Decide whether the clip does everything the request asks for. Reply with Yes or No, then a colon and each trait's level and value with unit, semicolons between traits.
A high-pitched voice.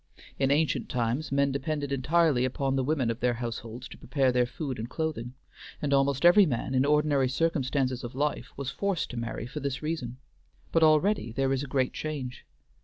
No: low, 135 Hz